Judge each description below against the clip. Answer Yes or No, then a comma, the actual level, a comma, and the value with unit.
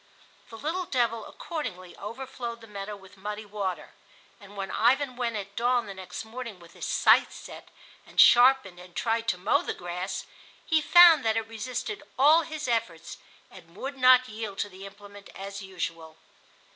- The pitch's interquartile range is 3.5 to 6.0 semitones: Yes, average, 4.6 semitones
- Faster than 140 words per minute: Yes, average, 170 wpm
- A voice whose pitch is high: Yes, high, 220 Hz